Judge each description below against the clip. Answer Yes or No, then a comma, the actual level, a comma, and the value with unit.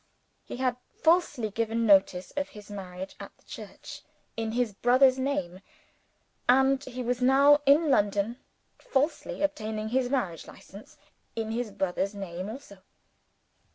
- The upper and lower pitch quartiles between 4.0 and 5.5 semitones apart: Yes, average, 4.7 semitones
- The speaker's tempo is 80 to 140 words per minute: Yes, slow, 135 wpm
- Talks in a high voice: Yes, high, 230 Hz